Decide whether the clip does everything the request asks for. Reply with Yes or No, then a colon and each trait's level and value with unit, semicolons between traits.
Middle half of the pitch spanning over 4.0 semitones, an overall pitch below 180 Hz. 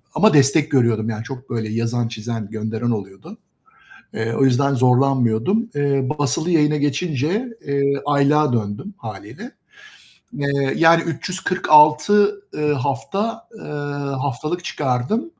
Yes: average, 4.9 semitones; medium, 140 Hz